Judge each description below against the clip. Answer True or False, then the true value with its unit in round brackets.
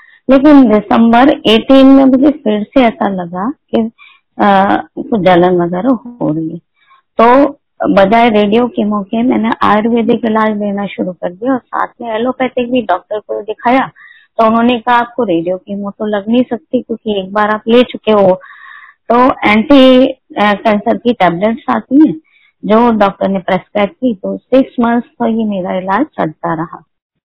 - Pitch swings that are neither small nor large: True (4.0 semitones)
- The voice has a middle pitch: False (230 Hz)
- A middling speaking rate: True (170 wpm)